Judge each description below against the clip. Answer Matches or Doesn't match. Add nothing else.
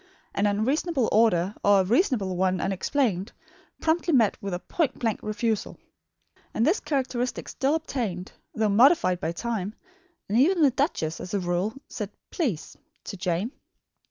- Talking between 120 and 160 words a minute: Matches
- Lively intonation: Matches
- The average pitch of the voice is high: Matches